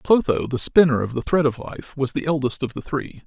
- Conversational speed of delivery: No, fast, 255 wpm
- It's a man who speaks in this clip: Yes, male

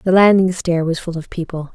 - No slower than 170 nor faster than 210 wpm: No, fast, 240 wpm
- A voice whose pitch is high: No, medium, 175 Hz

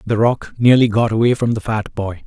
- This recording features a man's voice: Yes, male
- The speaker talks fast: Yes, fast, 240 wpm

